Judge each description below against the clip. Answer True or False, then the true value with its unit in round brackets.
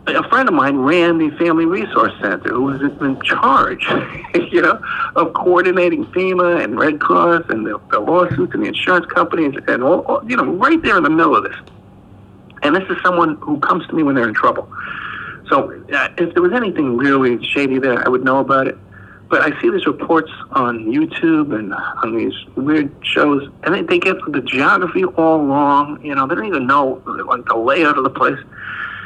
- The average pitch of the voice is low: False (170 Hz)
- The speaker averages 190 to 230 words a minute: True (205 wpm)